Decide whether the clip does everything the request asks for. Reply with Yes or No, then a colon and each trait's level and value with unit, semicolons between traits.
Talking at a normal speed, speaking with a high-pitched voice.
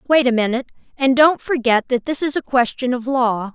No: fast, 220 wpm; very high, 255 Hz